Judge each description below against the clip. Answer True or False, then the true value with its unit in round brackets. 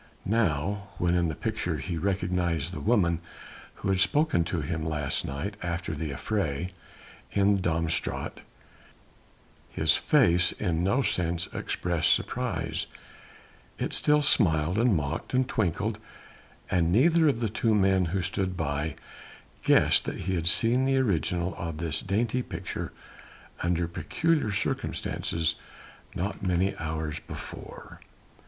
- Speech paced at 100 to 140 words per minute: True (135 wpm)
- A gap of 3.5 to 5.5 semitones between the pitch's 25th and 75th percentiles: True (4.1 semitones)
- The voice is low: True (90 Hz)